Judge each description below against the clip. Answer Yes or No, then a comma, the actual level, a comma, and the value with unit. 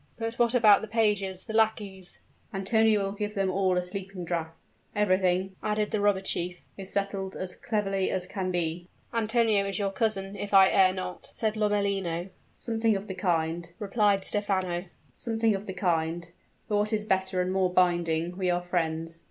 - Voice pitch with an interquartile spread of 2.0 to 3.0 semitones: Yes, narrow, 2.6 semitones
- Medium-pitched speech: No, high, 195 Hz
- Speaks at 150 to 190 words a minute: Yes, average, 170 wpm